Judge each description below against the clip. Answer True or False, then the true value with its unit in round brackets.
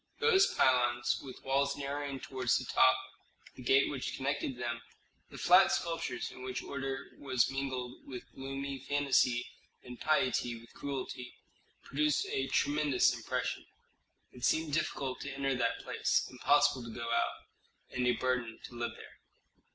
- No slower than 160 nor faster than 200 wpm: False (150 wpm)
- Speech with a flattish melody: True (2.1 semitones)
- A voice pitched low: True (130 Hz)